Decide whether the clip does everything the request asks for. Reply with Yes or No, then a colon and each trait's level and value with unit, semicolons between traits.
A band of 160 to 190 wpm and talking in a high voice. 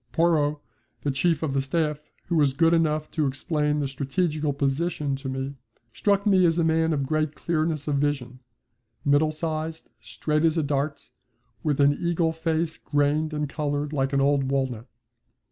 No: average, 170 wpm; medium, 150 Hz